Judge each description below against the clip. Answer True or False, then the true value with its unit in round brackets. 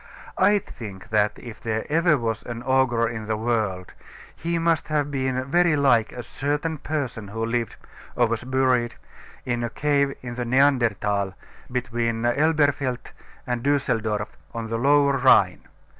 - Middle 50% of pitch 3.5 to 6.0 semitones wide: True (3.8 semitones)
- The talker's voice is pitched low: True (125 Hz)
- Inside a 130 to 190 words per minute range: True (150 wpm)